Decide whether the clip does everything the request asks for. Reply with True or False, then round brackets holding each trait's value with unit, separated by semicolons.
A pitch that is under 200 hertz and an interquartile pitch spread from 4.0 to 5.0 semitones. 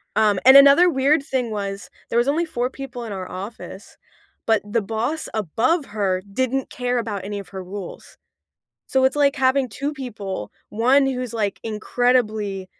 False (235 Hz; 4.6 semitones)